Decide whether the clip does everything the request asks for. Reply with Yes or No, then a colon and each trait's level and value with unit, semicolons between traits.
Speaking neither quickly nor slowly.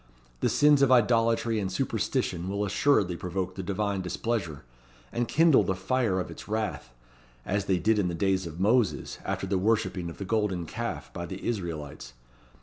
Yes: average, 175 wpm